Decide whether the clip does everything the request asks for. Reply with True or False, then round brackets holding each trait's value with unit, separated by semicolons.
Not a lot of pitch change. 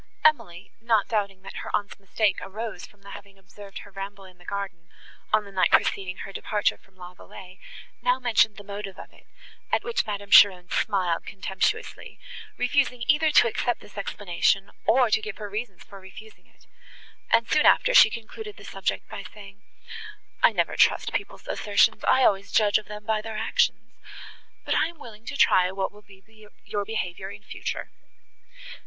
True (2.3 semitones)